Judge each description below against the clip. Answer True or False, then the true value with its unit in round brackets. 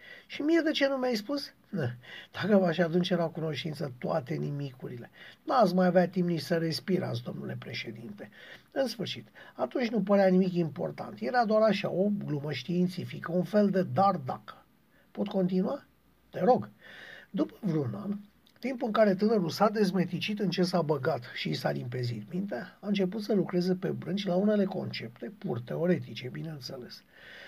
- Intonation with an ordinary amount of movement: True (3.7 semitones)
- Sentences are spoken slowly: False (165 wpm)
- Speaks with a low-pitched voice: False (185 Hz)